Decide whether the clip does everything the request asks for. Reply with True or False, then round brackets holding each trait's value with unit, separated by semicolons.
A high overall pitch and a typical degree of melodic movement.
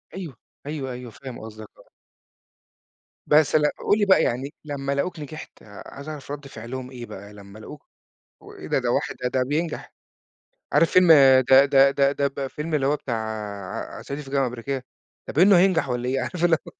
False (140 Hz; 3.5 semitones)